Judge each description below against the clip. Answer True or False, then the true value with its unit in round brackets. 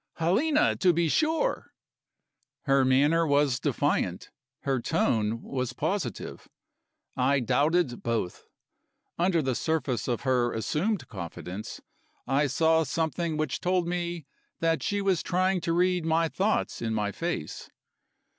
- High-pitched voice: False (155 Hz)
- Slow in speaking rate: True (125 wpm)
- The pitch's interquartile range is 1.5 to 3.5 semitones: False (5.5 semitones)